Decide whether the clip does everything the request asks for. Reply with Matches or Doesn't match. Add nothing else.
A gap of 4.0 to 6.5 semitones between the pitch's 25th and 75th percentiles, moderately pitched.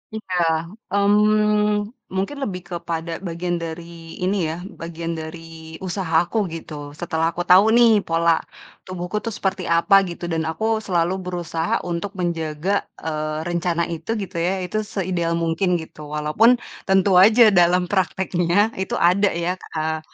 Doesn't match